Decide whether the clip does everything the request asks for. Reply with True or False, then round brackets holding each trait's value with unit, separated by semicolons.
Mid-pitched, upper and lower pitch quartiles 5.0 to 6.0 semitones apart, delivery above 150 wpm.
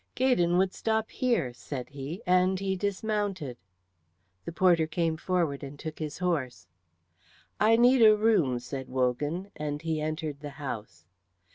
False (165 Hz; 5.5 semitones; 145 wpm)